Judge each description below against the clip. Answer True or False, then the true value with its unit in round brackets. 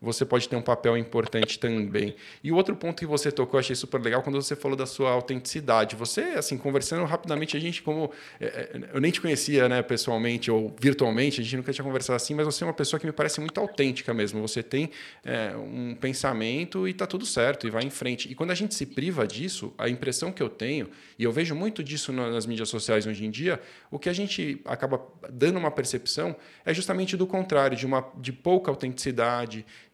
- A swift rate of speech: True (220 wpm)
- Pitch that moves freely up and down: False (4.5 semitones)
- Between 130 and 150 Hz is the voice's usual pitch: True (135 Hz)